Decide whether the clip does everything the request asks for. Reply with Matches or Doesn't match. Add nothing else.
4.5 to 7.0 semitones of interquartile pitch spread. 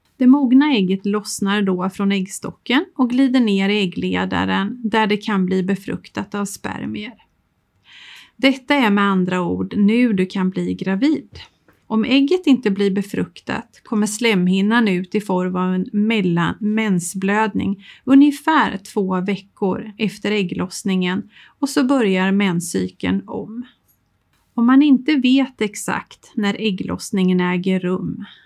Doesn't match